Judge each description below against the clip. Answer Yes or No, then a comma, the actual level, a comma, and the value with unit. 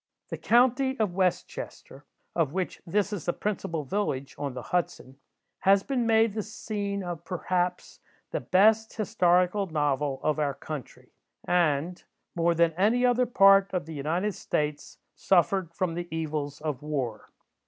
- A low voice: No, medium, 180 Hz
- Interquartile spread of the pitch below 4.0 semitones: No, average, 5.1 semitones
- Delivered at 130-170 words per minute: Yes, average, 155 wpm